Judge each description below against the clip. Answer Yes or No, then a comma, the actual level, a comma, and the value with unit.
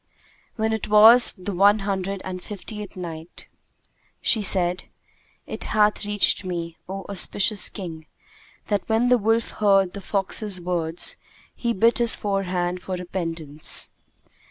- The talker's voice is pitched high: Yes, high, 195 Hz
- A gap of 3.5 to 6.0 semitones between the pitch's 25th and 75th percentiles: No, average, 2.9 semitones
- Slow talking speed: Yes, slow, 130 wpm